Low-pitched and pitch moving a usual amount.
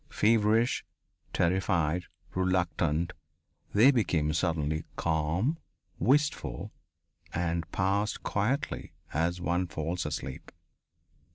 Yes: very low, 90 Hz; average, 4.4 semitones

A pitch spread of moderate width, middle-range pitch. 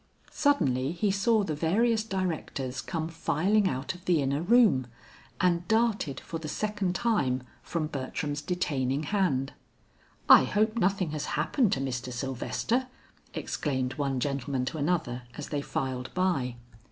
No: wide, 6.5 semitones; medium, 155 Hz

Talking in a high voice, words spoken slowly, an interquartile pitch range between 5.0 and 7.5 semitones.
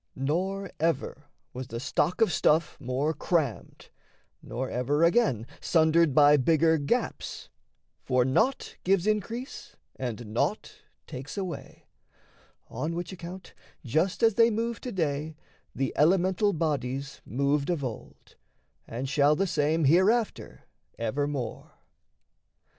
No: medium, 155 Hz; slow, 120 wpm; wide, 5.4 semitones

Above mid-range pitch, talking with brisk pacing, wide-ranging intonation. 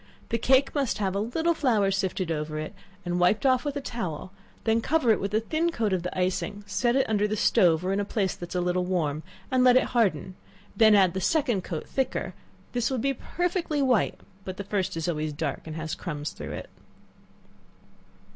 Yes: high, 205 Hz; fast, 215 wpm; wide, 5.8 semitones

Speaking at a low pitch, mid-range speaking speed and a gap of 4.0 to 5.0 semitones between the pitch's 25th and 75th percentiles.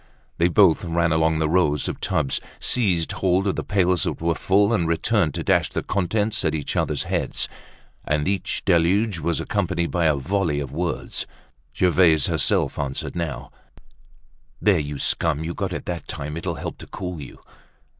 No: very low, 85 Hz; average, 175 wpm; average, 3.3 semitones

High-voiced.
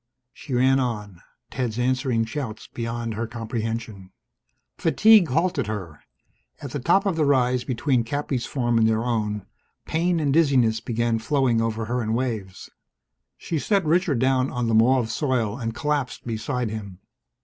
No: low, 120 Hz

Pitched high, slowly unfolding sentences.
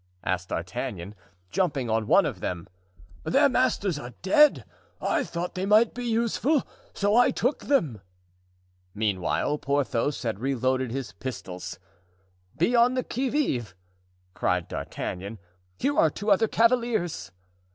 No: medium, 150 Hz; slow, 130 wpm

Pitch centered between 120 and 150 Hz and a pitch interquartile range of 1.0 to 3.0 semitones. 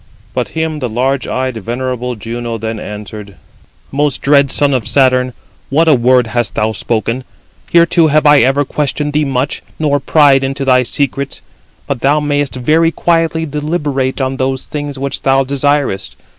Yes: low, 135 Hz; average, 2.7 semitones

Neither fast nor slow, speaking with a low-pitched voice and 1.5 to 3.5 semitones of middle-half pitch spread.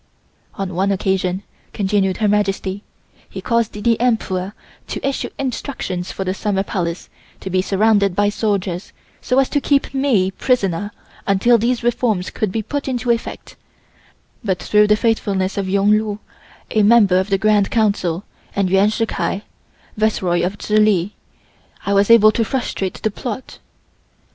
No: average, 155 wpm; high, 205 Hz; average, 2.9 semitones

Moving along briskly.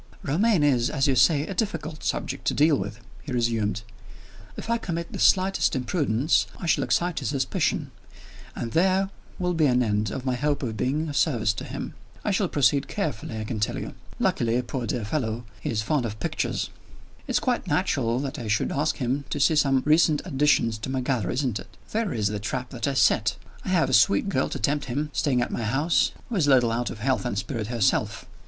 Yes: fast, 215 wpm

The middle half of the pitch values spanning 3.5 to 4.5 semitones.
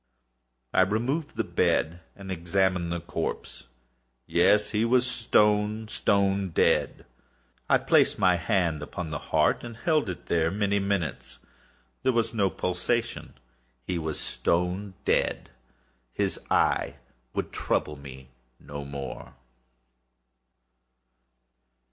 Yes: average, 4.1 semitones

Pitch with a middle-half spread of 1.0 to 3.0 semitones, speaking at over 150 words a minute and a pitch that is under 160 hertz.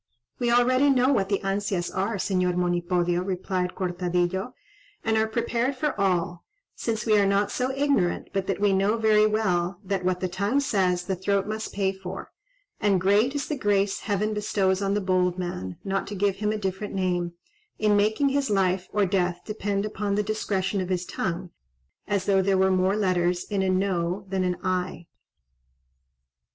No: narrow, 2.5 semitones; average, 185 wpm; high, 195 Hz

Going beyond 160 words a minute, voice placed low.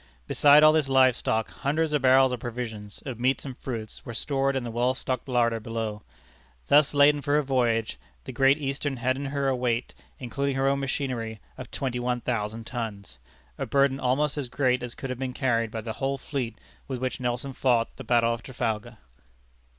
Yes: average, 200 wpm; low, 130 Hz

